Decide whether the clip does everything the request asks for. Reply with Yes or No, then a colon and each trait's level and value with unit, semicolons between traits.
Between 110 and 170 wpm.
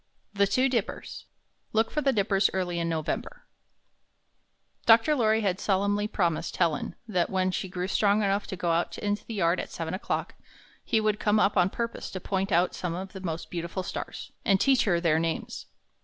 No: average, 190 wpm